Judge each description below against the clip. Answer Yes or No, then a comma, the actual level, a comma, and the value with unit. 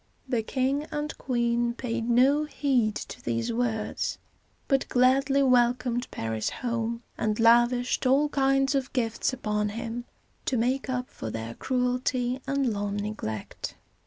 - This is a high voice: Yes, high, 245 Hz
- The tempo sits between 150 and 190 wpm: No, slow, 135 wpm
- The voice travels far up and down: No, average, 2.8 semitones